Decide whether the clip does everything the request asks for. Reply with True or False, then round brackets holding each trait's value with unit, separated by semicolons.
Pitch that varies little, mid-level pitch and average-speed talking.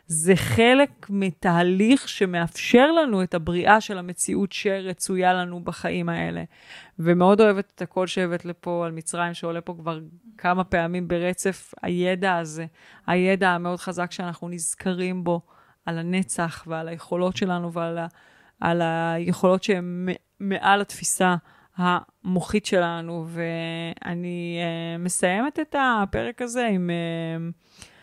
True (2.2 semitones; 180 Hz; 120 wpm)